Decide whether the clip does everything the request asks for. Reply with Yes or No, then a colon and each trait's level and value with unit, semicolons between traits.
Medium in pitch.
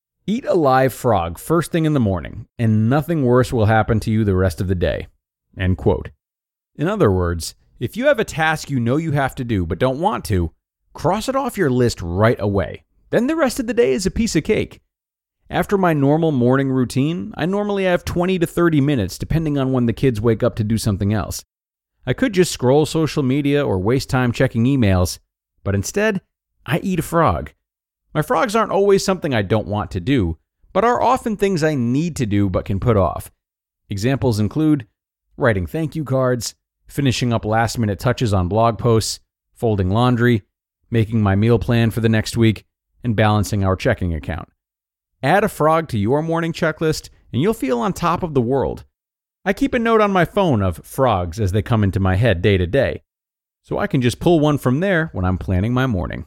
No: low, 125 Hz